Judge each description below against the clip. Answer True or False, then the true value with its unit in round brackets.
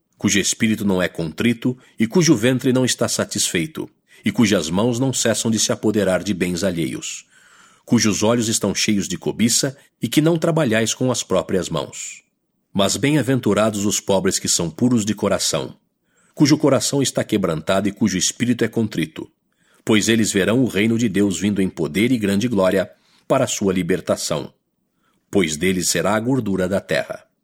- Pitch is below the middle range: True (110 Hz)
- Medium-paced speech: True (170 wpm)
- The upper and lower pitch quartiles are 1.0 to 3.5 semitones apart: False (4.2 semitones)